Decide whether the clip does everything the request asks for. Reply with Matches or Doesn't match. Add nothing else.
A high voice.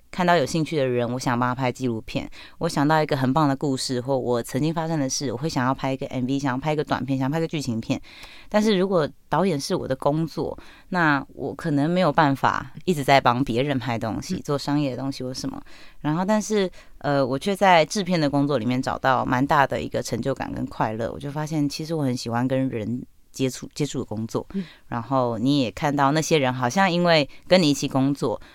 Doesn't match